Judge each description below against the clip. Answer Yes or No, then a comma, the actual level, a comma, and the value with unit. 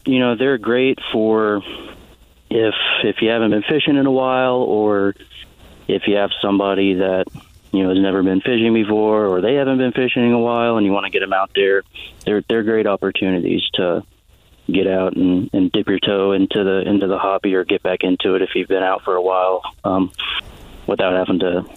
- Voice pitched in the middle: No, low, 100 Hz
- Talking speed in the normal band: No, fast, 210 wpm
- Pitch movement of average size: Yes, average, 3.2 semitones